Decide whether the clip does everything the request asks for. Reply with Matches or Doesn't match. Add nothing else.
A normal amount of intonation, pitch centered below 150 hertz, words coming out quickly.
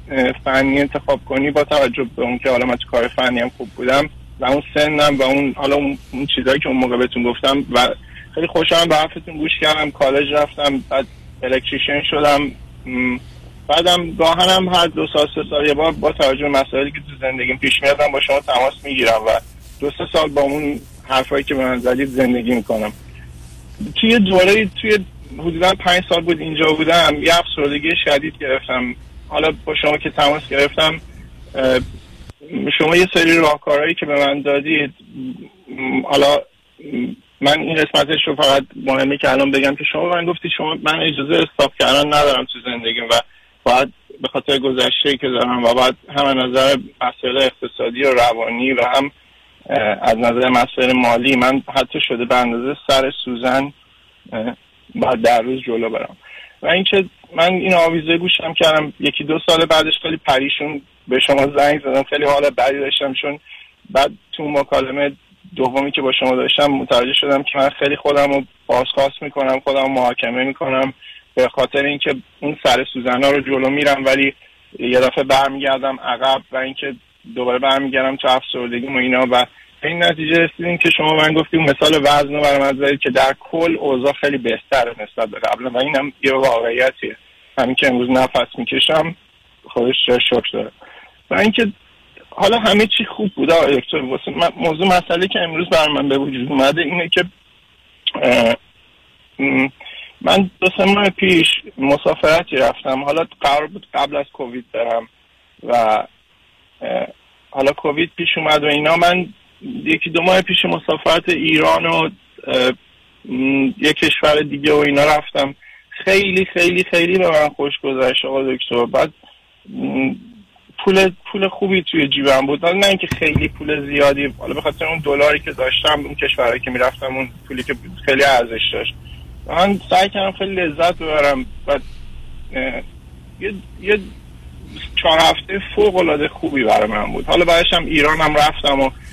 Matches